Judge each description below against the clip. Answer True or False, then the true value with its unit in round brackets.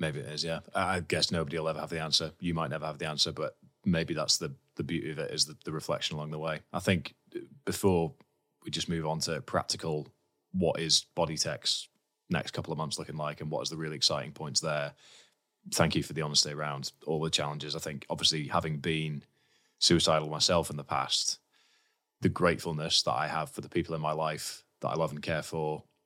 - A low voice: True (80 Hz)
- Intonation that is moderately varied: False (1.4 semitones)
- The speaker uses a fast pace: True (220 wpm)